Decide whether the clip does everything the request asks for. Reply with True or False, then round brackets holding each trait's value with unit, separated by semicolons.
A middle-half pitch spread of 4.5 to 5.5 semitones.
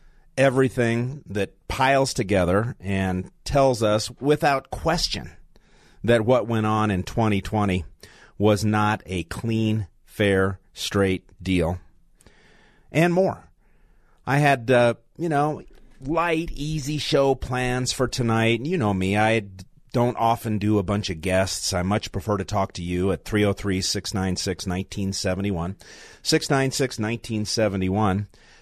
True (4.8 semitones)